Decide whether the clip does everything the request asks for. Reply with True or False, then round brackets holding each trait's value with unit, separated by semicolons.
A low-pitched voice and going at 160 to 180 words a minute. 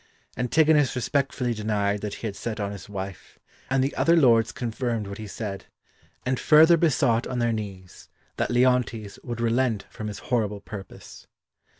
True (115 Hz; 170 wpm)